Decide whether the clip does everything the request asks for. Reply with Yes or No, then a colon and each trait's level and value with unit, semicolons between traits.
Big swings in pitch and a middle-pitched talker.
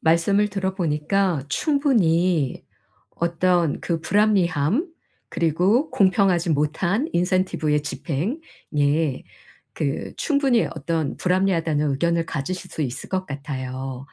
No: average, 4.4 semitones; medium, 170 Hz